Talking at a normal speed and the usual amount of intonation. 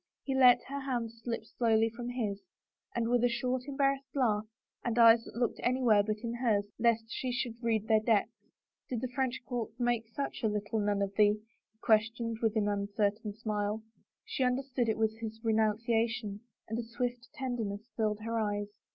No: average, 185 wpm; narrow, 2.3 semitones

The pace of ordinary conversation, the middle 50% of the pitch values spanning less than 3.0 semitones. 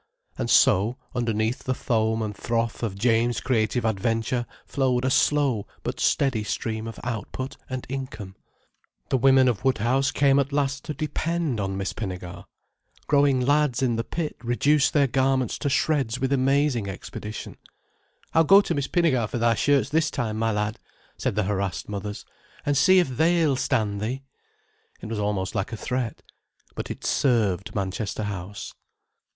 No: average, 160 wpm; average, 4.2 semitones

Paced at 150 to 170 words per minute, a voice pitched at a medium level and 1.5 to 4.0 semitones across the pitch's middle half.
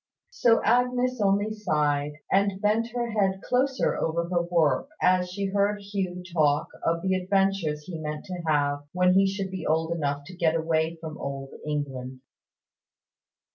No: average, 160 wpm; medium, 180 Hz; average, 4.5 semitones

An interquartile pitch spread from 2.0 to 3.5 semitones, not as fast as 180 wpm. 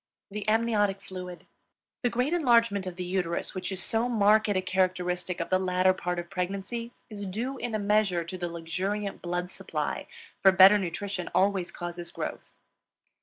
Yes: average, 2.7 semitones; average, 170 wpm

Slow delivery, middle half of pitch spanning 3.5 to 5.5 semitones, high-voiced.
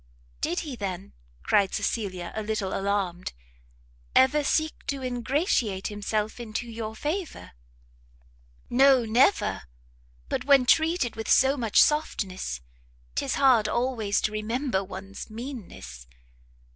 Yes: slow, 115 wpm; average, 4.9 semitones; high, 225 Hz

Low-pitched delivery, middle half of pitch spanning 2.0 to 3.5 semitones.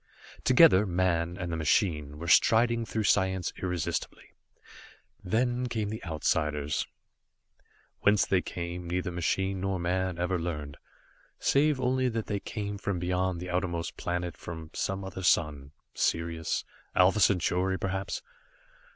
Yes: very low, 90 Hz; narrow, 2.6 semitones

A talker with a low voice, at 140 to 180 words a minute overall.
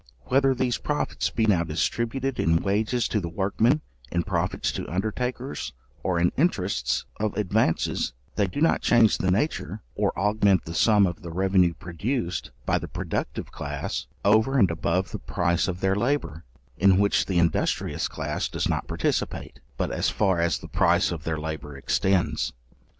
Yes: very low, 95 Hz; average, 165 wpm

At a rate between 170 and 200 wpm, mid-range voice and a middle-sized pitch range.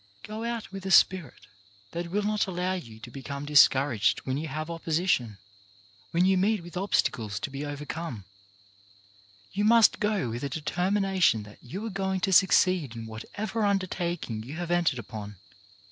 No: average, 175 wpm; medium, 170 Hz; wide, 6.7 semitones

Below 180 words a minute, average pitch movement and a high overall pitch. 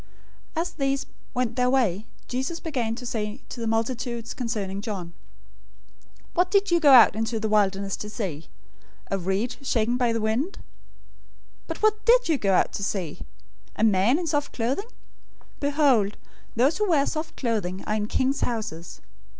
Yes: average, 170 wpm; average, 4.9 semitones; high, 235 Hz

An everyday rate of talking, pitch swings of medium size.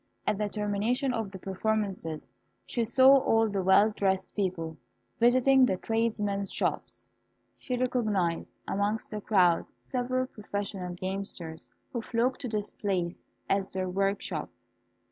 No: slow, 130 wpm; average, 3.4 semitones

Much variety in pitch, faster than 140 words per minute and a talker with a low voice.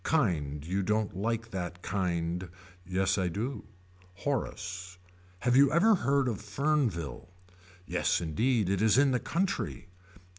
No: wide, 6.7 semitones; slow, 135 wpm; low, 100 Hz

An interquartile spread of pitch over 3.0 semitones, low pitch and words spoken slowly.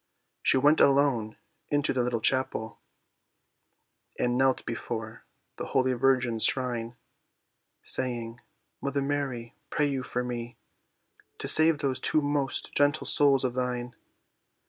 No: narrow, 2.6 semitones; low, 130 Hz; slow, 125 wpm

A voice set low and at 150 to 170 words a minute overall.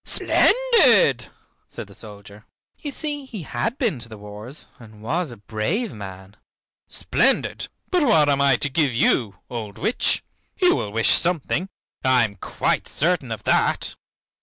Yes: low, 130 Hz; average, 155 wpm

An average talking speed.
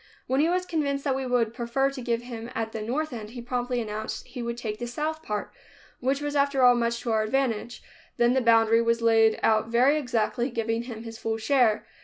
No: fast, 230 wpm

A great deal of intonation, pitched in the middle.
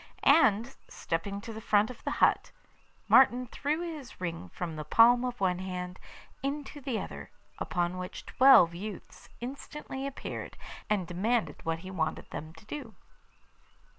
No: wide, 6.2 semitones; high, 210 Hz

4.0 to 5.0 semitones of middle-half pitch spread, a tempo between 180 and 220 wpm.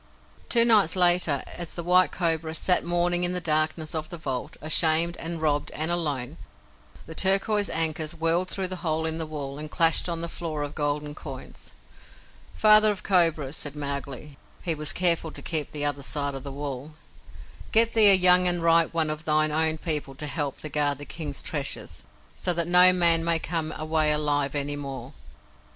No: average, 2.9 semitones; average, 190 wpm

